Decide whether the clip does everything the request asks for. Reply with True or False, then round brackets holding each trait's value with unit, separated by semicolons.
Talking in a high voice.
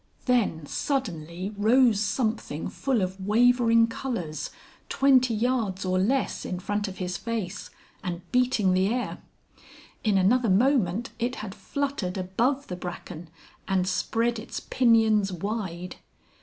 True (210 Hz)